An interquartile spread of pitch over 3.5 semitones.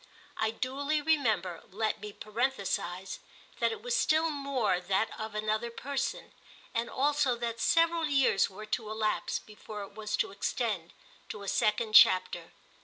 Yes: average, 5.0 semitones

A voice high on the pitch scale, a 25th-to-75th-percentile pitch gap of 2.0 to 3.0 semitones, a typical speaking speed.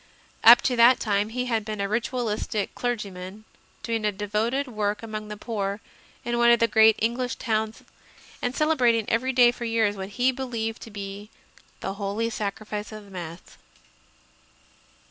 Yes: high, 220 Hz; narrow, 2.5 semitones; average, 165 wpm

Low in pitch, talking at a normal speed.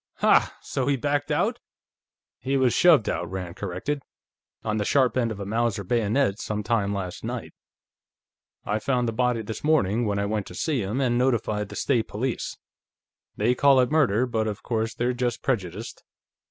Yes: low, 115 Hz; average, 180 wpm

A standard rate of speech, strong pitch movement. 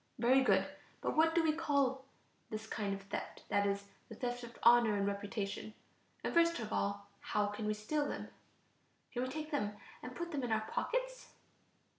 Yes: average, 190 wpm; wide, 5.9 semitones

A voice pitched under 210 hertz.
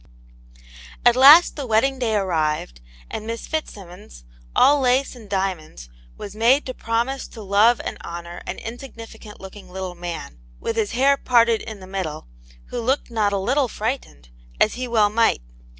No: high, 220 Hz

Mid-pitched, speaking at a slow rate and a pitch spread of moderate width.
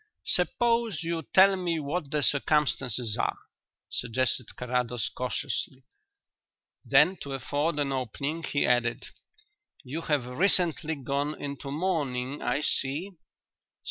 Yes: medium, 145 Hz; slow, 110 wpm; average, 4.2 semitones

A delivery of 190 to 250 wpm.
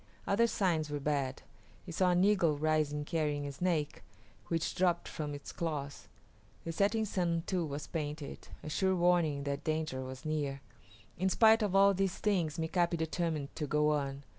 No: average, 170 wpm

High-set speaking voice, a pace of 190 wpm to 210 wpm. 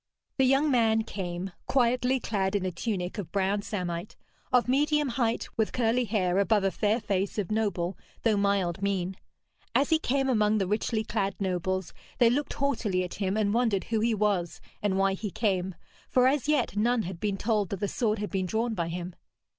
Yes: high, 210 Hz; average, 195 wpm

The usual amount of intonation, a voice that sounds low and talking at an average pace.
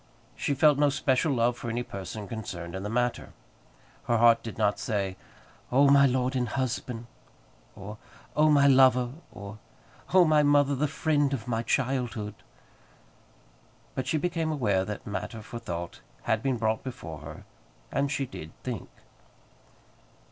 Yes: average, 4.5 semitones; low, 125 Hz; average, 155 wpm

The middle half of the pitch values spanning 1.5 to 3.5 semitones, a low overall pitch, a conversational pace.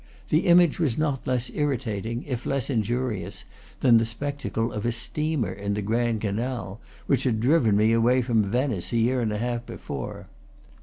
Yes: average, 3.2 semitones; low, 120 Hz; average, 175 wpm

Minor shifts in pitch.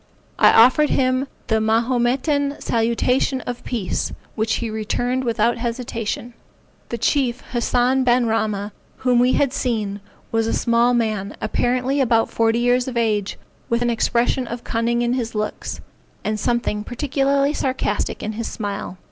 Yes: narrow, 2.1 semitones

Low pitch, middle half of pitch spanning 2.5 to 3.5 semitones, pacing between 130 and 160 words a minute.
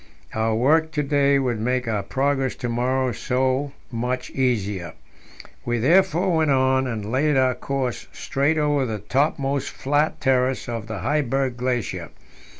Yes: low, 130 Hz; average, 2.8 semitones; average, 150 wpm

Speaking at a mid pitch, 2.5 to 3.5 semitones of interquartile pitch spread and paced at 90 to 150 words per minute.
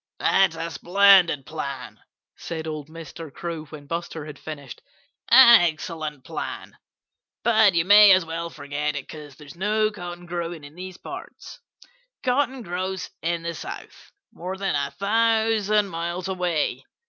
No: medium, 170 Hz; average, 4.0 semitones; average, 145 wpm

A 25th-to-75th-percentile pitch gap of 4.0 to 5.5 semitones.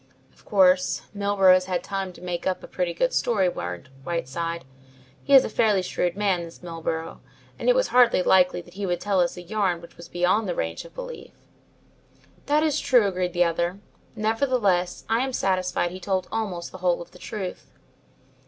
No: average, 3.1 semitones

